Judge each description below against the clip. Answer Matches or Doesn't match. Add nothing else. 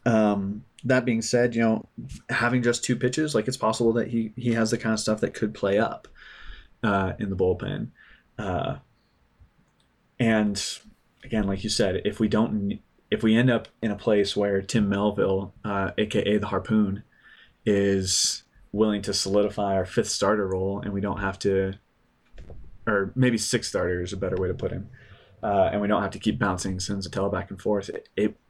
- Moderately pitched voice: Doesn't match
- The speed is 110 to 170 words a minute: Doesn't match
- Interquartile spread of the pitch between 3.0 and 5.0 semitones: Doesn't match